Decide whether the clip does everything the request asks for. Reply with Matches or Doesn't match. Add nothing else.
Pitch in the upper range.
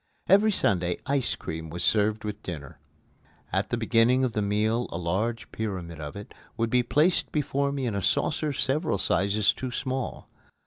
Doesn't match